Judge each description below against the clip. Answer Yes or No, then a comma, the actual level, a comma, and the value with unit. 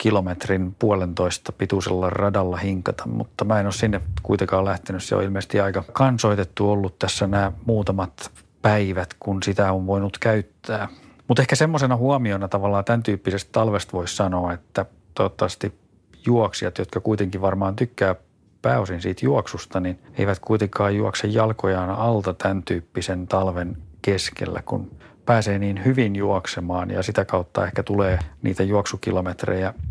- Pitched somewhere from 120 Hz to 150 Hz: No, low, 100 Hz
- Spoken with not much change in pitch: Yes, narrow, 2.3 semitones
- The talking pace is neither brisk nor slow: Yes, average, 140 wpm